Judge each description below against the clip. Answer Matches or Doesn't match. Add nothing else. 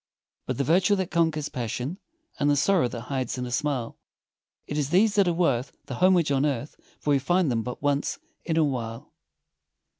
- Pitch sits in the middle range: Matches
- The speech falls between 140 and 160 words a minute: Doesn't match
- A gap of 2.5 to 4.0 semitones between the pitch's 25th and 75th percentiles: Doesn't match